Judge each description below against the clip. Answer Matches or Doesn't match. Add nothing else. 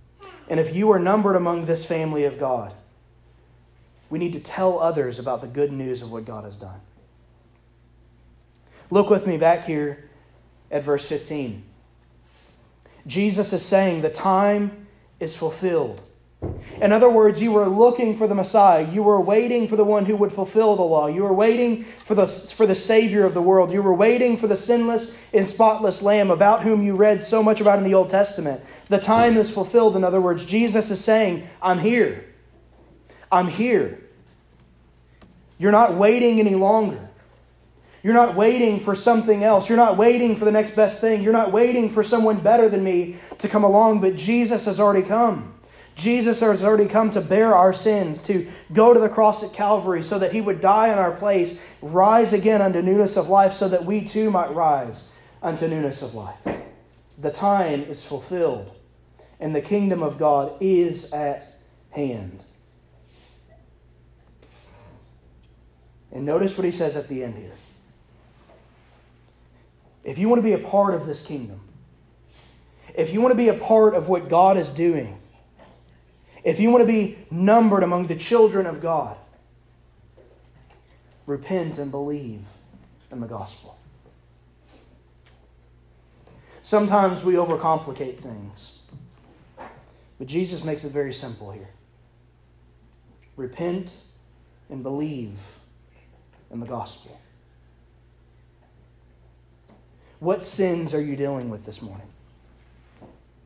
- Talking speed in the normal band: Matches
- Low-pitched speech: Doesn't match